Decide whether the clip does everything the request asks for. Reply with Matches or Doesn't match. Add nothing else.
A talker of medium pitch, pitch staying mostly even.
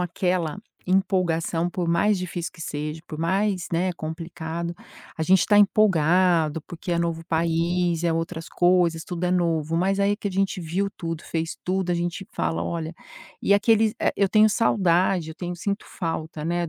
Matches